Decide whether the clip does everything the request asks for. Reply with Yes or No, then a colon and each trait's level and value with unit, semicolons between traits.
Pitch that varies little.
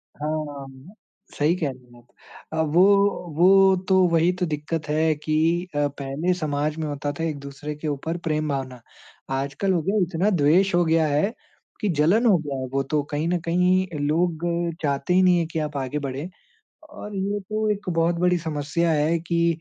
No: average, 3.5 semitones